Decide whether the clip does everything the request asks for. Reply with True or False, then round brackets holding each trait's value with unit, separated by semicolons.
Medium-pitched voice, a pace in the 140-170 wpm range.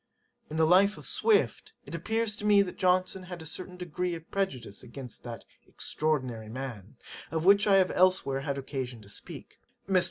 False (170 Hz; 185 wpm)